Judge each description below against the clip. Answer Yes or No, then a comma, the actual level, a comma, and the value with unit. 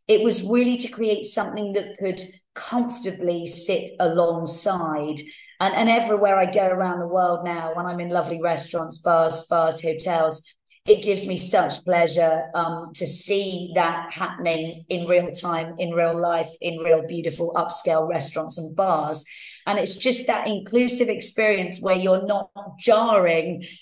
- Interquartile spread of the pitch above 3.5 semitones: No, average, 3.2 semitones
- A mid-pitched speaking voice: Yes, medium, 175 Hz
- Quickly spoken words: No, average, 155 wpm